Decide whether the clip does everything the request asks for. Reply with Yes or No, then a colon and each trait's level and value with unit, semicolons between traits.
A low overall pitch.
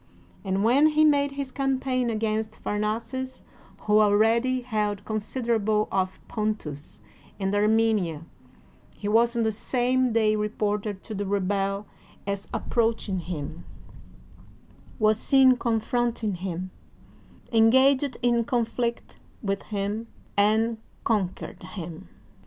No: high, 220 Hz